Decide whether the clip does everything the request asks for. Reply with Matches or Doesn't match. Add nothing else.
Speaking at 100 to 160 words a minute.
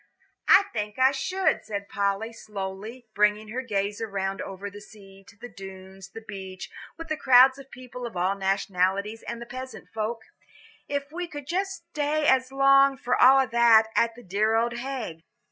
Doesn't match